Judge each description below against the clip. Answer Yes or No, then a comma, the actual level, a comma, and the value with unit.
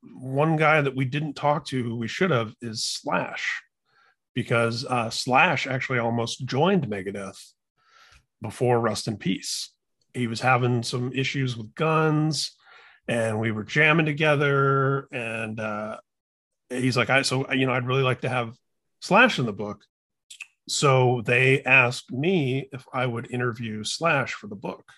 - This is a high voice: No, low, 125 Hz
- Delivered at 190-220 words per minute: No, average, 155 wpm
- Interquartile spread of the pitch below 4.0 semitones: Yes, average, 2.7 semitones